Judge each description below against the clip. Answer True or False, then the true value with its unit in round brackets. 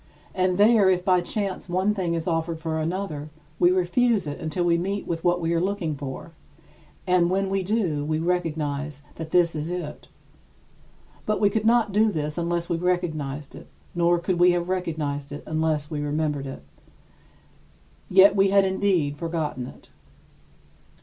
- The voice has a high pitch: False (175 Hz)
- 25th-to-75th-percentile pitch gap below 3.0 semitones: False (3.4 semitones)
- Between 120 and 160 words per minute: False (170 wpm)